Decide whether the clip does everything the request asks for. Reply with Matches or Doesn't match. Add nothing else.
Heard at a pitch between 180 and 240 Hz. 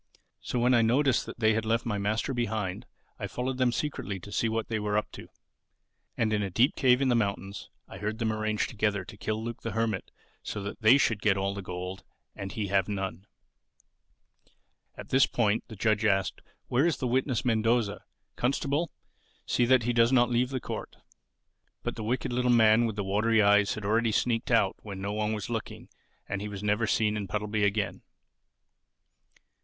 Doesn't match